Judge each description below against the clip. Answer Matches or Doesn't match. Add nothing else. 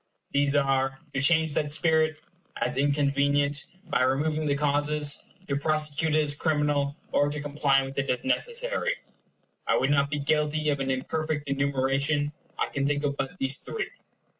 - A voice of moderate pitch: Matches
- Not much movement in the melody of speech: Matches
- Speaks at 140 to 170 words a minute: Matches